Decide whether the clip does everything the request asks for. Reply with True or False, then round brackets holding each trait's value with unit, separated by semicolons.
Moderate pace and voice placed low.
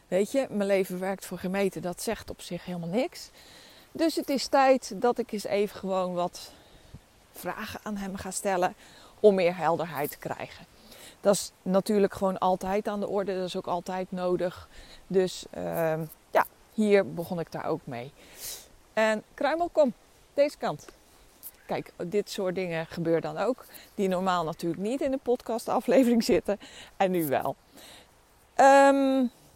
False (160 wpm; 195 Hz)